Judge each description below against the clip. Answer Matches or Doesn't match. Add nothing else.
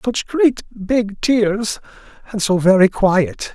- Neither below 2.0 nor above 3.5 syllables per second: Matches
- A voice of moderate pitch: Doesn't match